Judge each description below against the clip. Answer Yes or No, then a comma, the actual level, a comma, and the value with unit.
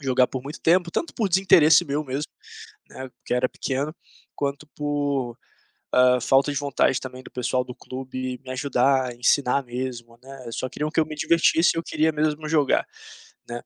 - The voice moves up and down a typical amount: Yes, average, 3.0 semitones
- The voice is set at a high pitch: No, low, 135 Hz